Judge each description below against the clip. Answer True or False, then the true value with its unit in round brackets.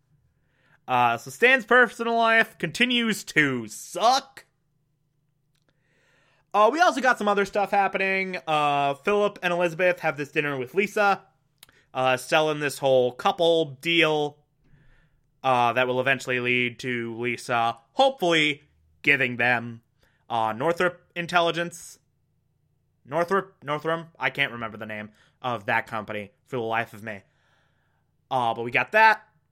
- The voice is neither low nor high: True (145 Hz)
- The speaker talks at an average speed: False (130 wpm)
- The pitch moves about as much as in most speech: False (5.8 semitones)